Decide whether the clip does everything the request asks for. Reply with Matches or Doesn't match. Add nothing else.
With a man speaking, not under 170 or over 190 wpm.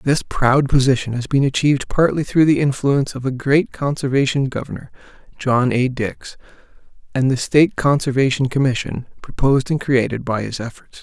Doesn't match